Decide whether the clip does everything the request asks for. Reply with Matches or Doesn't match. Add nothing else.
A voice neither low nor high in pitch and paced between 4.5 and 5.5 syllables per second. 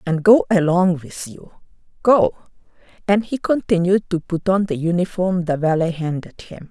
Matches